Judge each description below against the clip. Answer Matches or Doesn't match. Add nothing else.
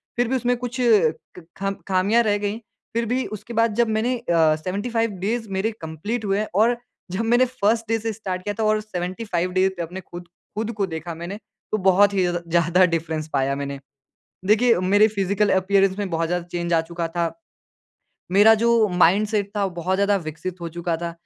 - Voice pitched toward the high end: Matches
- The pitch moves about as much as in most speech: Matches